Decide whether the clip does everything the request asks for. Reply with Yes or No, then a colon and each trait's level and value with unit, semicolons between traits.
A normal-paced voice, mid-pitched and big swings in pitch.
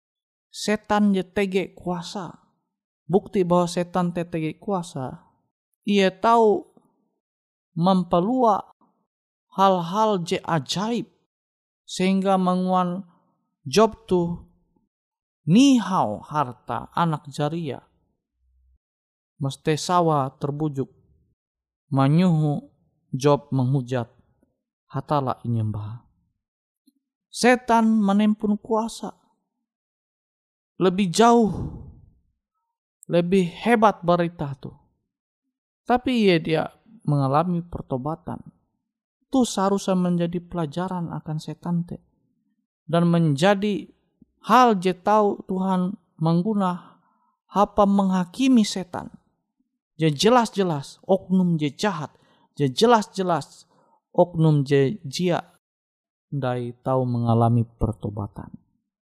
No: slow, 75 wpm; medium, 180 Hz; wide, 6.0 semitones